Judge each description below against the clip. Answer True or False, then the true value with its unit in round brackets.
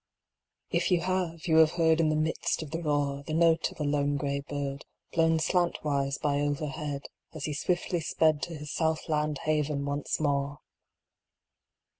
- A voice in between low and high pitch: True (150 Hz)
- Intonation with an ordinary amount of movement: False (2.2 semitones)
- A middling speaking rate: True (170 wpm)